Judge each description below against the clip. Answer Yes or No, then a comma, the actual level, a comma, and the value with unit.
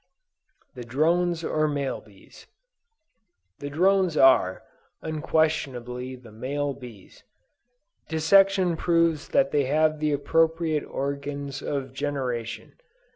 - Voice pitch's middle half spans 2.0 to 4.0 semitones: Yes, average, 3.4 semitones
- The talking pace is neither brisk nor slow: No, slow, 100 wpm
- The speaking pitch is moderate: Yes, medium, 145 Hz